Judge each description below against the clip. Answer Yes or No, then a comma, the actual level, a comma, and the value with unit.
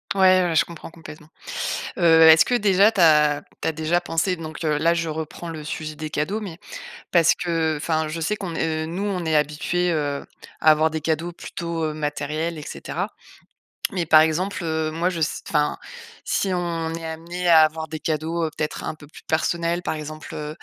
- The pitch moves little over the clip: Yes, narrow, 1.8 semitones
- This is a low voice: No, medium, 160 Hz